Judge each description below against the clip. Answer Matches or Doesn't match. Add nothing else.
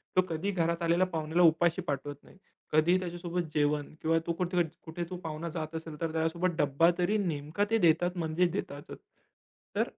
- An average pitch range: Doesn't match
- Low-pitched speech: Doesn't match